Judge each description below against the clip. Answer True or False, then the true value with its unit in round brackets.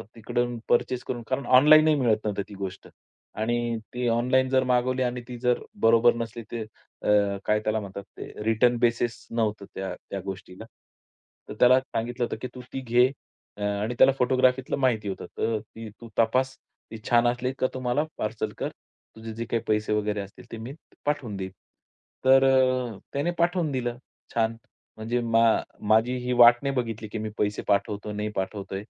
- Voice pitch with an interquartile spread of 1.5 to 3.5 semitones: True (3.0 semitones)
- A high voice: False (115 Hz)